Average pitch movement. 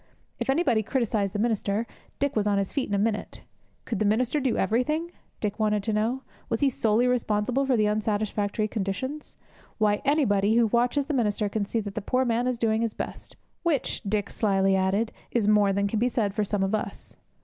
Yes: average, 3.2 semitones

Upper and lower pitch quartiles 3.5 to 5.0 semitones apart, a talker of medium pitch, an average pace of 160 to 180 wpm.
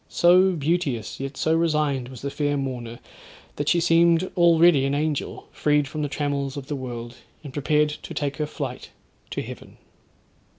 No: average, 3.0 semitones; medium, 145 Hz; average, 170 wpm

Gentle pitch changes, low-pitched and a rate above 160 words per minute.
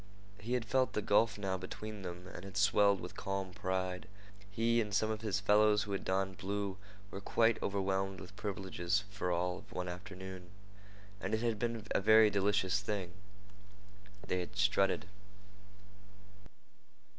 No: narrow, 2.0 semitones; low, 100 Hz; average, 155 wpm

